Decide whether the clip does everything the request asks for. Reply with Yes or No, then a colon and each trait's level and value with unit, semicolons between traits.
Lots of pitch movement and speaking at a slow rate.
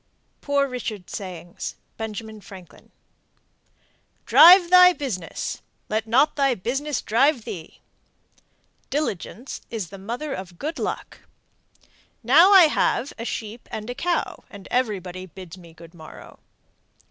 Yes: wide, 7.1 semitones; slow, 120 wpm